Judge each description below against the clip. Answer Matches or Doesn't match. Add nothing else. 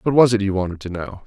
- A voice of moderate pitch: Doesn't match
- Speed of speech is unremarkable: Doesn't match